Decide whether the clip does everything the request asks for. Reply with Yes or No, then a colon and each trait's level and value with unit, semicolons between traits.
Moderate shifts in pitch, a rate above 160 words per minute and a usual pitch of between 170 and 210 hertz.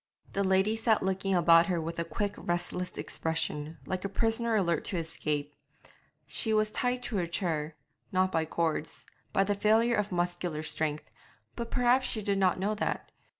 Yes: average, 4.2 semitones; average, 175 wpm; medium, 185 Hz